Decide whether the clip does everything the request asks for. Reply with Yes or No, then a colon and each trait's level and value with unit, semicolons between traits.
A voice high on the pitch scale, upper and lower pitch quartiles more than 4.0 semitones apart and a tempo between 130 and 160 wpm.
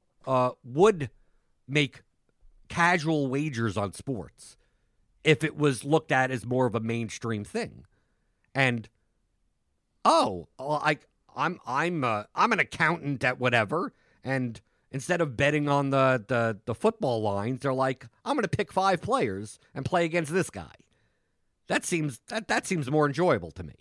No: low, 135 Hz; average, 5.0 semitones; average, 150 wpm